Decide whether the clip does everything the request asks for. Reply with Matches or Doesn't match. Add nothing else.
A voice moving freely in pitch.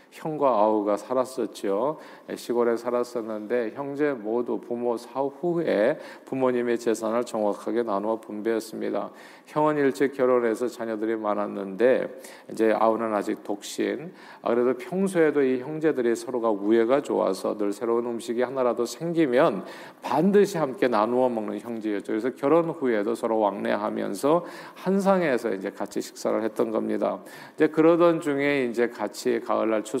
Doesn't match